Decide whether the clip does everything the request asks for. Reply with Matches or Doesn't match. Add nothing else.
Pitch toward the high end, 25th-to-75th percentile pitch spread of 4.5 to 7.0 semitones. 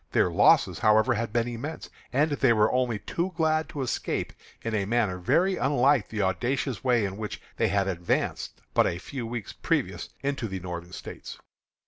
Doesn't match